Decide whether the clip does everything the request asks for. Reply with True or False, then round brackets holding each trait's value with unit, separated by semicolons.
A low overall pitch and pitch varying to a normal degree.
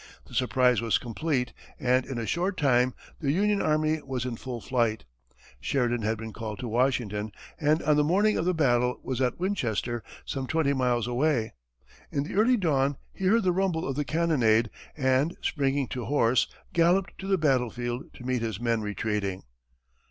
True (130 Hz; 4.7 semitones)